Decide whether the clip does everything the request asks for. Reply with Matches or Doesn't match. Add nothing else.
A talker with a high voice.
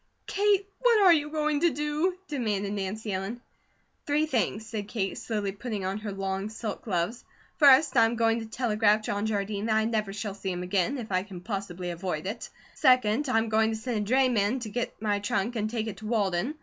Matches